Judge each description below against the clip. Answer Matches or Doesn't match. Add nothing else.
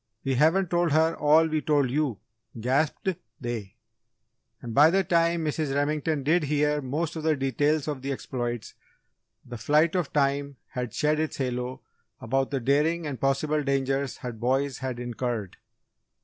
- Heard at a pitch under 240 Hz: Matches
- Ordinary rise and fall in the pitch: Matches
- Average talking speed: Matches